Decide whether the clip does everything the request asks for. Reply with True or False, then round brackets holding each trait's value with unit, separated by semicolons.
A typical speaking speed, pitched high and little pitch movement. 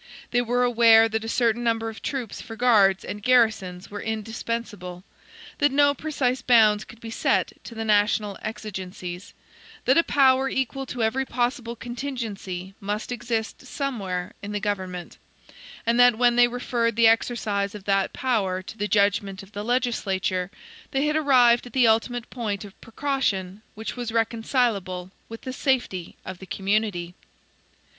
False (160 wpm; 225 Hz; 3.5 semitones)